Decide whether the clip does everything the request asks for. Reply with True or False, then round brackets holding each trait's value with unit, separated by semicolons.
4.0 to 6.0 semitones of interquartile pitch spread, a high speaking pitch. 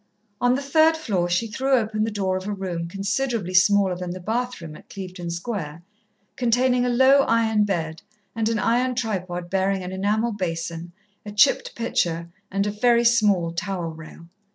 True (4.8 semitones; 200 Hz)